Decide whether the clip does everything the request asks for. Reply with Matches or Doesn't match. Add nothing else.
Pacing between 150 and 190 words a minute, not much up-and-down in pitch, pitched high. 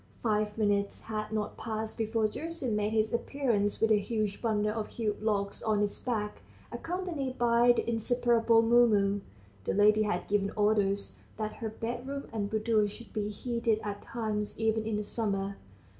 Matches